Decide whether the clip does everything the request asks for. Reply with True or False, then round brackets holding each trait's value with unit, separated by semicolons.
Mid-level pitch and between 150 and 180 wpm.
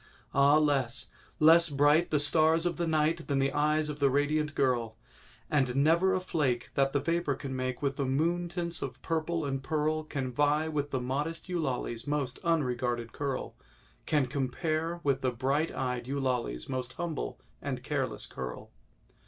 True (145 Hz; 165 wpm)